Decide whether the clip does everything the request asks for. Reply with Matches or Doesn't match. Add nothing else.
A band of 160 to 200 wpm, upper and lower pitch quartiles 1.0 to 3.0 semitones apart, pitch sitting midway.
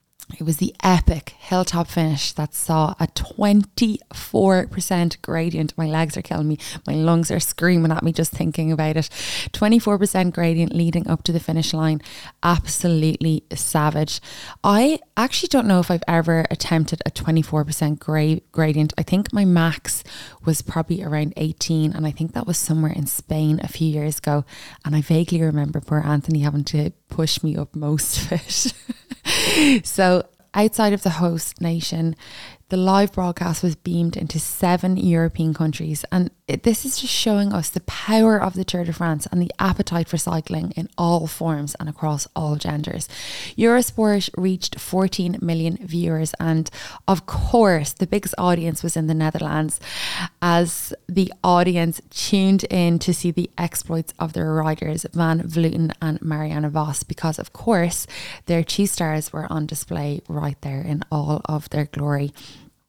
Matches